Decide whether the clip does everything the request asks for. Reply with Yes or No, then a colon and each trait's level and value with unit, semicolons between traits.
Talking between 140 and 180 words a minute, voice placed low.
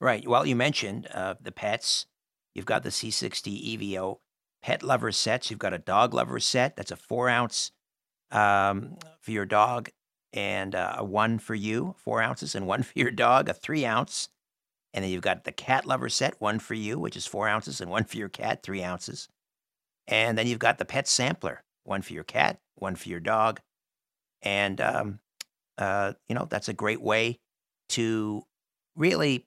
No: average, 190 wpm; low, 105 Hz